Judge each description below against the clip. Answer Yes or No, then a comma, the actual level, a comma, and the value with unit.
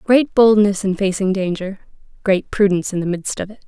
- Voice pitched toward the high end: Yes, high, 195 Hz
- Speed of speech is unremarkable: Yes, average, 195 wpm